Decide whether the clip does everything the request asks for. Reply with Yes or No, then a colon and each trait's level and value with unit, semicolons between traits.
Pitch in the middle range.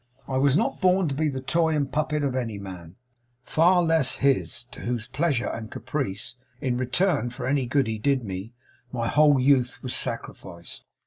No: low, 130 Hz